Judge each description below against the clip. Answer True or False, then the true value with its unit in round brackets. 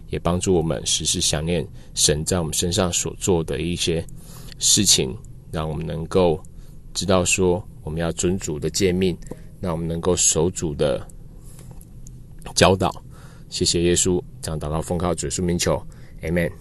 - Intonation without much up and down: True (2.3 semitones)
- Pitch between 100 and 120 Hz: False (85 Hz)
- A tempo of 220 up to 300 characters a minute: True (230 characters per minute)